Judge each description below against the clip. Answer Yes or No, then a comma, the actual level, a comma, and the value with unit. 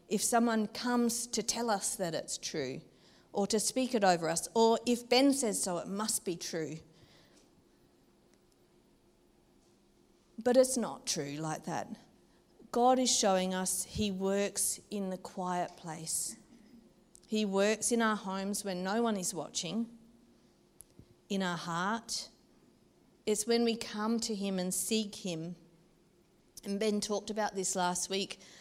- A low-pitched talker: No, high, 205 Hz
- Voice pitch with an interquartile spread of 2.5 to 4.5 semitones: Yes, average, 4.0 semitones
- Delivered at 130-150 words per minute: Yes, average, 145 wpm